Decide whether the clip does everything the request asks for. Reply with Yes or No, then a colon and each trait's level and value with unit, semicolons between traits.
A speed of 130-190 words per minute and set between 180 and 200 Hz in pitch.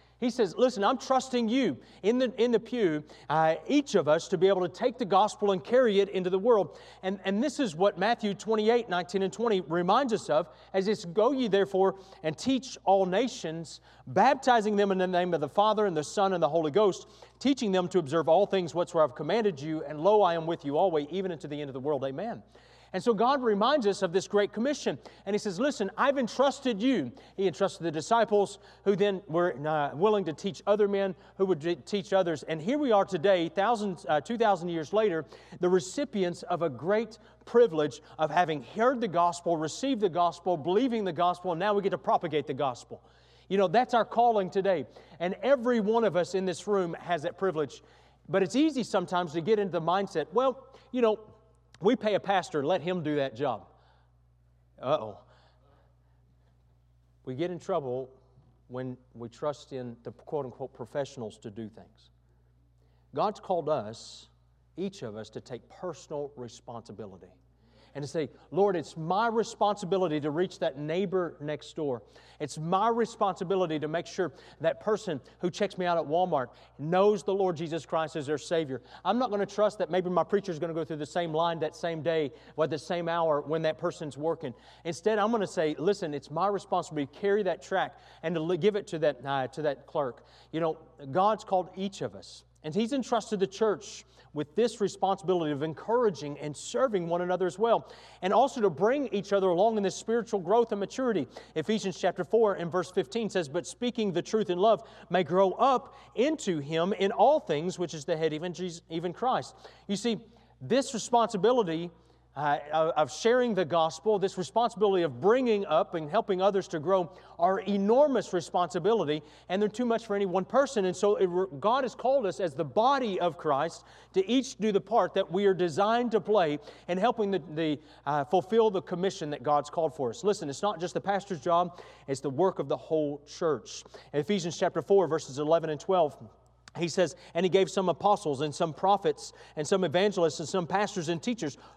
No: fast, 205 wpm; medium, 185 Hz